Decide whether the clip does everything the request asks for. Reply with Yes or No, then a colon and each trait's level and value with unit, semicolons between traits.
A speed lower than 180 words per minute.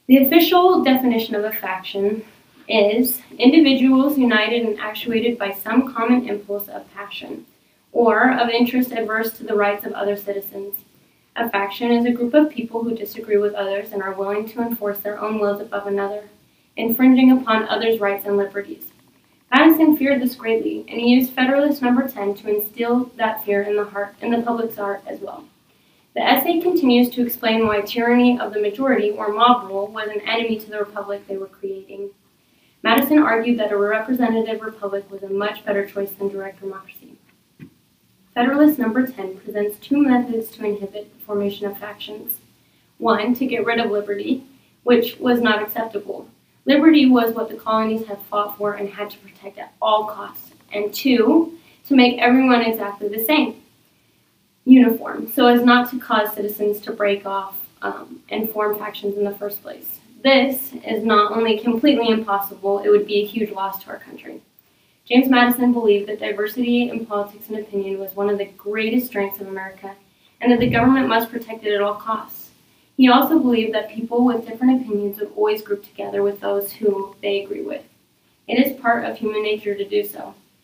No: average, 185 wpm